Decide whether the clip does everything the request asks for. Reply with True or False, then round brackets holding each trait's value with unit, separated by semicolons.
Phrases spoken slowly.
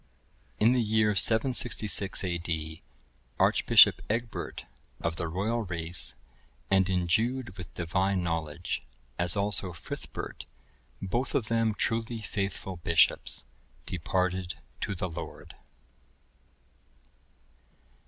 True (100 wpm)